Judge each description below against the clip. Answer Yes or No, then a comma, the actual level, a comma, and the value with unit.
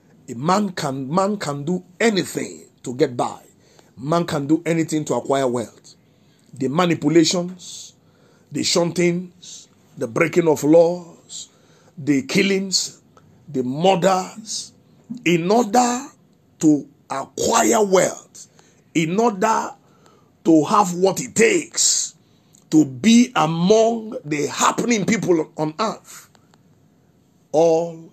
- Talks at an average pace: No, slow, 105 wpm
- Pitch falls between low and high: Yes, medium, 175 Hz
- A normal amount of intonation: Yes, average, 3.8 semitones